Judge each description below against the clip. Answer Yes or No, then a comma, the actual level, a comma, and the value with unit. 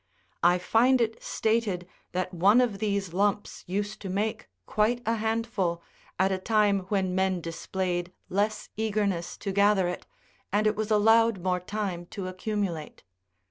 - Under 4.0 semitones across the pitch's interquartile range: Yes, average, 2.8 semitones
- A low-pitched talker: No, high, 200 Hz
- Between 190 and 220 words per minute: No, average, 150 wpm